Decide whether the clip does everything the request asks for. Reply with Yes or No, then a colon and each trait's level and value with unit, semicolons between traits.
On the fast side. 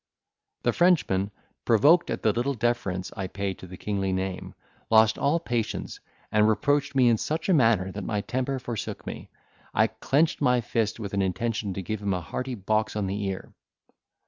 No: average, 185 wpm